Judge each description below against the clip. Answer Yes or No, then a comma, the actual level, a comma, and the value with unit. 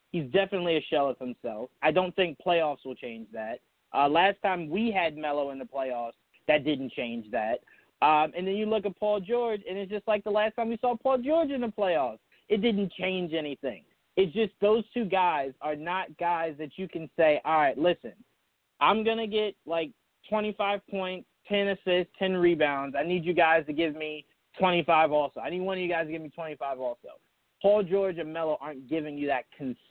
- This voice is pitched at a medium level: Yes, medium, 175 Hz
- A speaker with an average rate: No, fast, 215 wpm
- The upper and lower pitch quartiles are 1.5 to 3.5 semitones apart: No, average, 5.1 semitones